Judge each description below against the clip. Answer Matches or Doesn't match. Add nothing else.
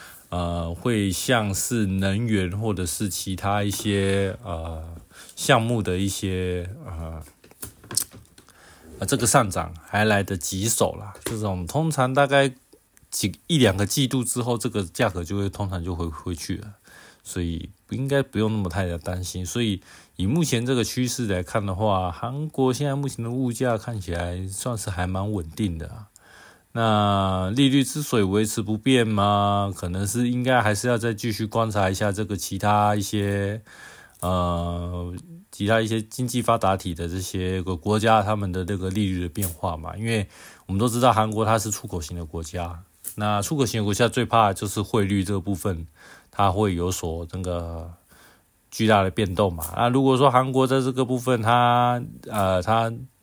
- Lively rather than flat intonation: Doesn't match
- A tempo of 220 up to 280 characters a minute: Matches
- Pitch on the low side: Matches